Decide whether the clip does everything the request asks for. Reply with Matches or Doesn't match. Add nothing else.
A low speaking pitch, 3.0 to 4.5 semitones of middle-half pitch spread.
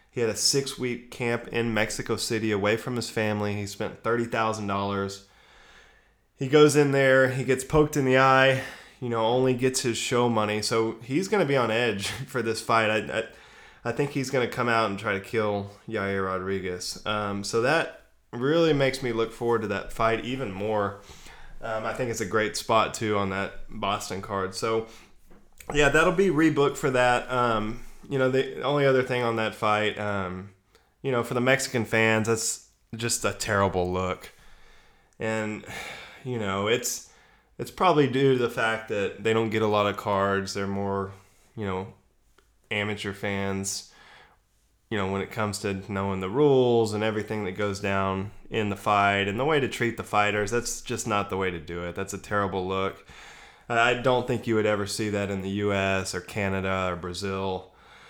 Matches